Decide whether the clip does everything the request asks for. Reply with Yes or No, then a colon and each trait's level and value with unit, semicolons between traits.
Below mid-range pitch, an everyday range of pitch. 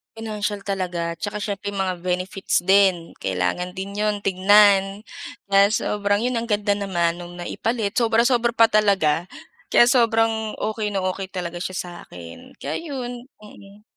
No: high, 200 Hz; average, 3.0 semitones